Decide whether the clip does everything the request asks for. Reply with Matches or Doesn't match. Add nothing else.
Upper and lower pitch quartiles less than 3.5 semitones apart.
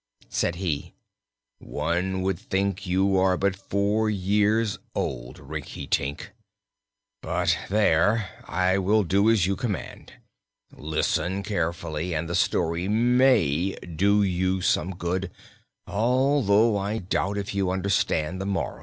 Matches